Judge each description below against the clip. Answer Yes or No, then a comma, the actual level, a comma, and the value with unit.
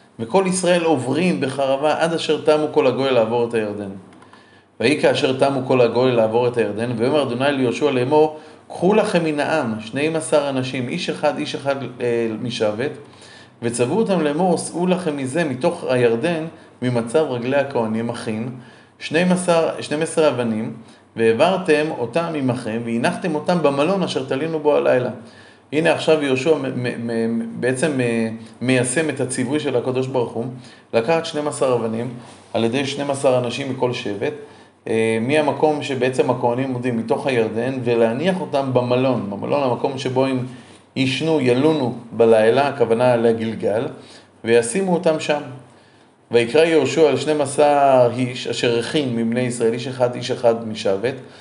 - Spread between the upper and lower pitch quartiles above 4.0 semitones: Yes, average, 4.4 semitones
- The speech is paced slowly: No, average, 140 wpm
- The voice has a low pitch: Yes, low, 130 Hz